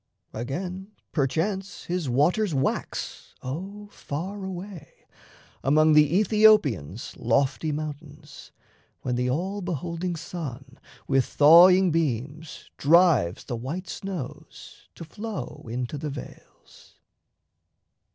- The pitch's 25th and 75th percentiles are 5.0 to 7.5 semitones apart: Yes, average, 5.3 semitones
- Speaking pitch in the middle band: Yes, medium, 155 Hz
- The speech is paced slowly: Yes, slow, 100 wpm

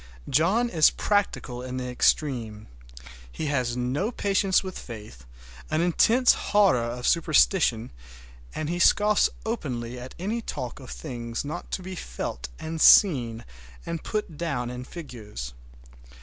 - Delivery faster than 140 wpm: No, slow, 135 wpm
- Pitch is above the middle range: No, medium, 145 Hz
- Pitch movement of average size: No, wide, 7.3 semitones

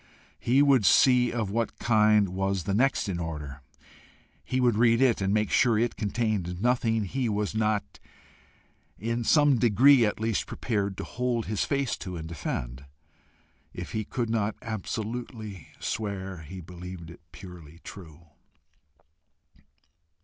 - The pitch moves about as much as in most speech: Yes, average, 4.1 semitones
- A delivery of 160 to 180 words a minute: No, average, 140 wpm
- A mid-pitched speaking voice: No, low, 105 Hz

